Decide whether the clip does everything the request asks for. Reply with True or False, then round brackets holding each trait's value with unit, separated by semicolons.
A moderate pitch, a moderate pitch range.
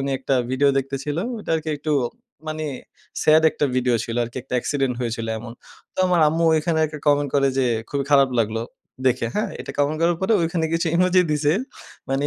True (145 Hz; 3.3 semitones)